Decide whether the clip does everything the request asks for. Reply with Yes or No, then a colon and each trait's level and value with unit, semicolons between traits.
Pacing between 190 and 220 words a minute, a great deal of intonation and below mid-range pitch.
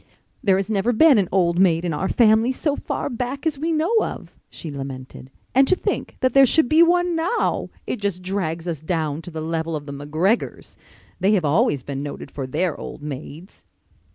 No: fast, 205 wpm; wide, 8.6 semitones; medium, 185 Hz